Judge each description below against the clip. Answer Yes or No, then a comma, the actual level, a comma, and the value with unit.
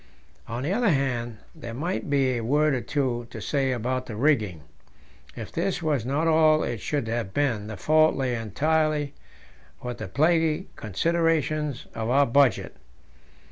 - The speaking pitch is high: No, medium, 140 Hz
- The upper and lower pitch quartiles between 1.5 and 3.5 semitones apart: No, average, 4.6 semitones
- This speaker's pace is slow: No, average, 160 wpm